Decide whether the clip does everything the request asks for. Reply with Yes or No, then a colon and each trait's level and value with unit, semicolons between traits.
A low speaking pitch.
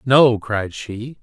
Yes: low, 115 Hz